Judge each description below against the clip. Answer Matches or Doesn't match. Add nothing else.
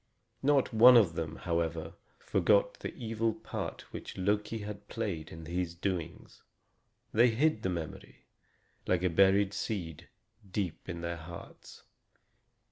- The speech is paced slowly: Matches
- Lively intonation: Doesn't match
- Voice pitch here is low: Matches